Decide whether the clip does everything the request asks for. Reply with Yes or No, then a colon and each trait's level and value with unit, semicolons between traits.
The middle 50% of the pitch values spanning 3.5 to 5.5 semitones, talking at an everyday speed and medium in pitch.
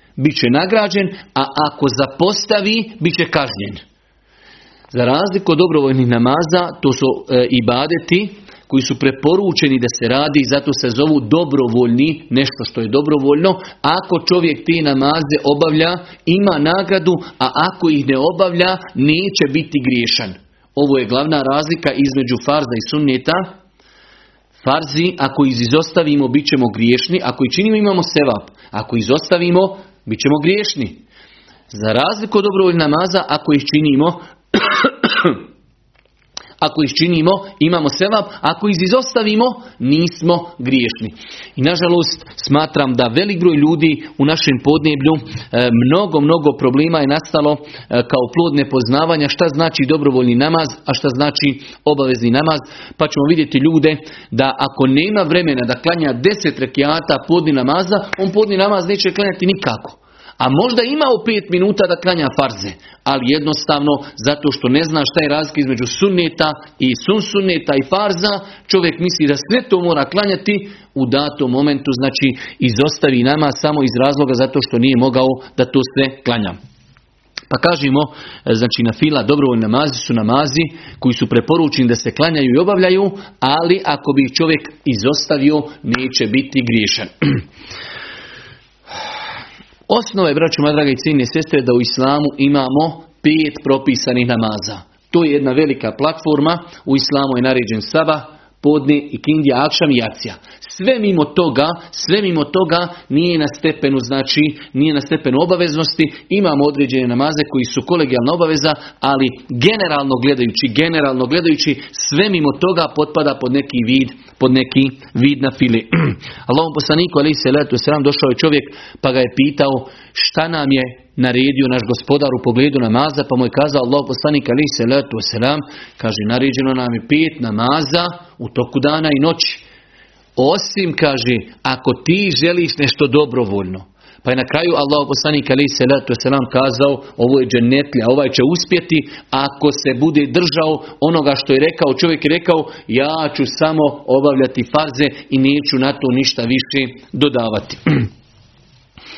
Yes: average, 3.8 semitones; average, 145 wpm; medium, 145 Hz